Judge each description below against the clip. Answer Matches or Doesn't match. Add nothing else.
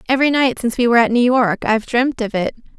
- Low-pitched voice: Doesn't match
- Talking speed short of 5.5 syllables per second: Doesn't match